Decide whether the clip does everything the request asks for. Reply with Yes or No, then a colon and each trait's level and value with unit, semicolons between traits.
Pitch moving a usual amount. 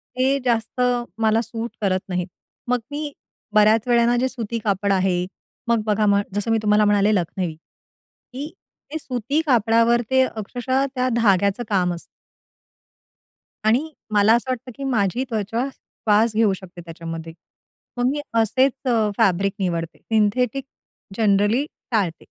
Yes: average, 3.7 semitones